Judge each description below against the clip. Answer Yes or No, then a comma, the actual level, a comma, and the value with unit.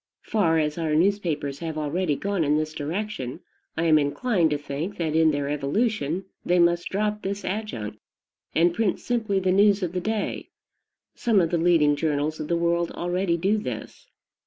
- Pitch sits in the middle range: Yes, medium, 170 Hz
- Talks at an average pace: Yes, average, 180 wpm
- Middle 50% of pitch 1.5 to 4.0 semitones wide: No, average, 4.6 semitones